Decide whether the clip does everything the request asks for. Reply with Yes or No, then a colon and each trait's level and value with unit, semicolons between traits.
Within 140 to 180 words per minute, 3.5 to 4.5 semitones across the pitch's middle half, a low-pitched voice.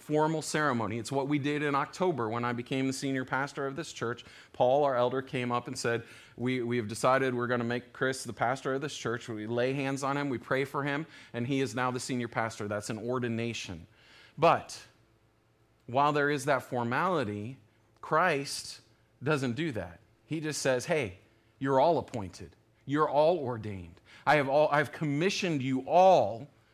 No: average, 190 wpm; average, 3.8 semitones; low, 125 Hz